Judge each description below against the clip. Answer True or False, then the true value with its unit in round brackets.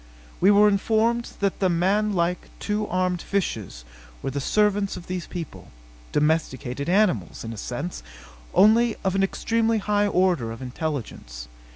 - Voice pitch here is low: False (185 Hz)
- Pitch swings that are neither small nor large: False (6.4 semitones)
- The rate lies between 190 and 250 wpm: False (145 wpm)